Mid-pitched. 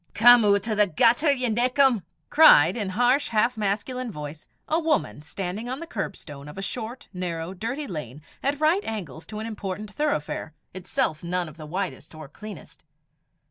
No: high, 210 Hz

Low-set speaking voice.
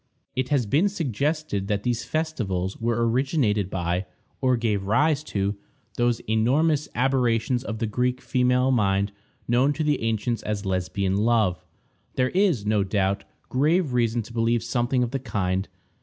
Yes: low, 120 Hz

